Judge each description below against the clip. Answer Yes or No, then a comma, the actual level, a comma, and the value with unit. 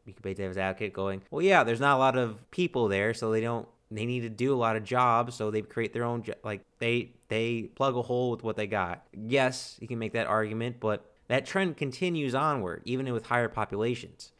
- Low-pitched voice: Yes, low, 115 Hz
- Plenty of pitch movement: No, average, 2.8 semitones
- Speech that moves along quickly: Yes, fast, 240 wpm